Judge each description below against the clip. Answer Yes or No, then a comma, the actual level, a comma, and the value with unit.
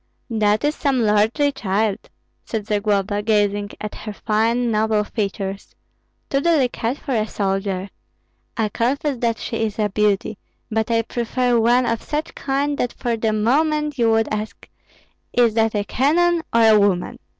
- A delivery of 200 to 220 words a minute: No, average, 160 wpm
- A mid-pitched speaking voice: No, high, 225 Hz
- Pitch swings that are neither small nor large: Yes, average, 3.0 semitones